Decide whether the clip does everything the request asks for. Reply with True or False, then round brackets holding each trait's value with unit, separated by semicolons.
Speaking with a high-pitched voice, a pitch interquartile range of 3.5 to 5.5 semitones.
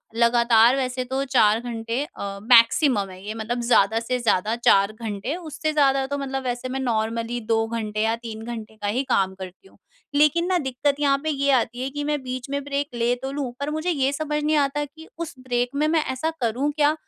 True (250 Hz; 3.8 semitones)